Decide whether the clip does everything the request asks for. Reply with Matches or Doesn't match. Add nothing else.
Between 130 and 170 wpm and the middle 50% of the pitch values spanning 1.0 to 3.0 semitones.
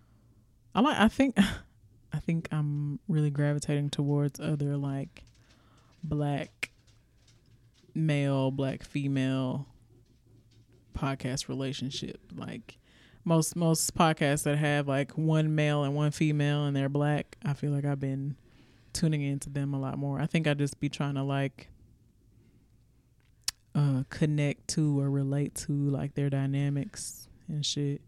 Matches